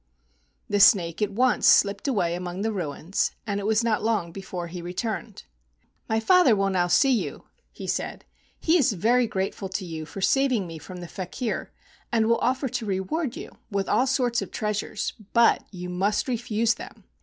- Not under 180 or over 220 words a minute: Yes, average, 185 wpm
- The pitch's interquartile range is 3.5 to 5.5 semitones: Yes, average, 4.4 semitones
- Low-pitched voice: No, high, 205 Hz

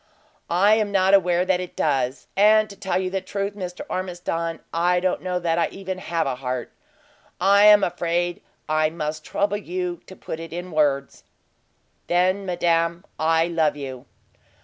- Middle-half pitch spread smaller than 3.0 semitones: Yes, narrow, 2.4 semitones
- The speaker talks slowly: No, average, 170 wpm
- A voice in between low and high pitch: Yes, medium, 175 Hz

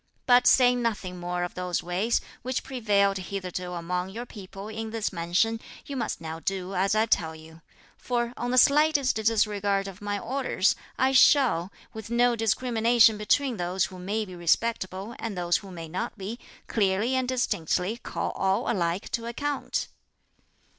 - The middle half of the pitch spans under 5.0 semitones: Yes, average, 4.5 semitones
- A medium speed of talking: Yes, average, 165 wpm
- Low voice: No, high, 205 Hz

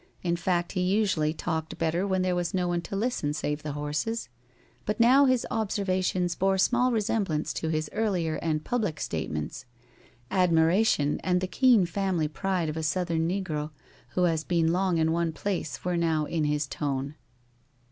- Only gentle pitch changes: No, average, 3.5 semitones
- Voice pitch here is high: No, medium, 175 Hz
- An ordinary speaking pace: Yes, average, 170 wpm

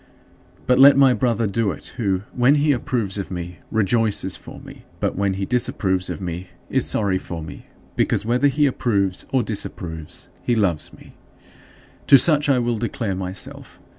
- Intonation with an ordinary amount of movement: Yes, average, 4.9 semitones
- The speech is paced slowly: No, average, 175 wpm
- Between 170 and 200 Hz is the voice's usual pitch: No, low, 110 Hz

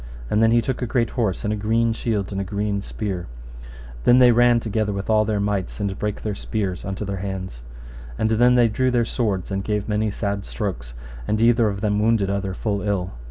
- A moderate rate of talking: No, fast, 225 wpm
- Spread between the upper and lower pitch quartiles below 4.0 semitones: Yes, narrow, 2.5 semitones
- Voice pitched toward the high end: No, low, 105 Hz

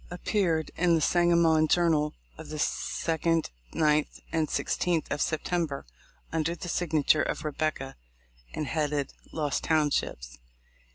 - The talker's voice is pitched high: No, medium, 155 Hz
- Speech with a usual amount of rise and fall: No, narrow, 2.1 semitones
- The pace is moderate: No, slow, 120 wpm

